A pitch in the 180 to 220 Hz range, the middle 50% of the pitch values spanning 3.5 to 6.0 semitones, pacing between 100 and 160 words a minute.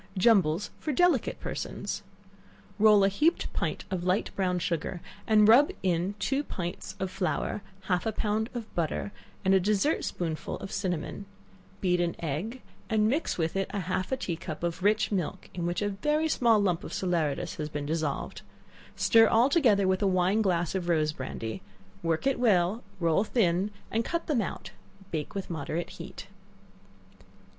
No: high, 190 Hz; average, 4.1 semitones; average, 170 wpm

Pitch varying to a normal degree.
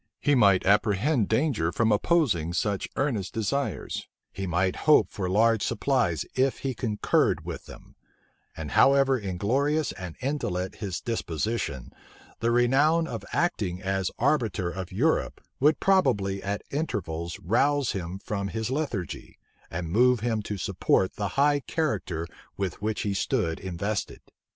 No: wide, 6.2 semitones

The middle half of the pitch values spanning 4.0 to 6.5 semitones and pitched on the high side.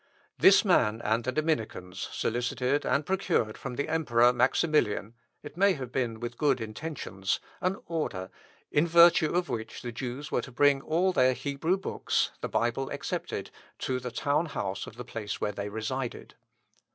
No: average, 5.2 semitones; low, 130 Hz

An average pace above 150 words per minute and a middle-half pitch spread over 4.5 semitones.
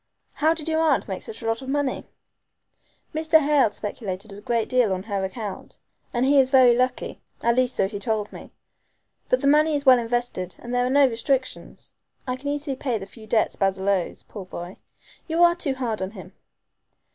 Yes: fast, 205 wpm; average, 5.2 semitones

